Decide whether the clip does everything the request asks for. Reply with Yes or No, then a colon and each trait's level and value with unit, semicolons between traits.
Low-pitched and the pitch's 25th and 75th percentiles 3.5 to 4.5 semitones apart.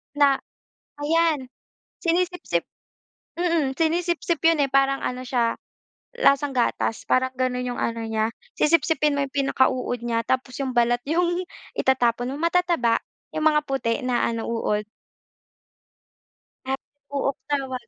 No: very high, 270 Hz; average, 4.2 semitones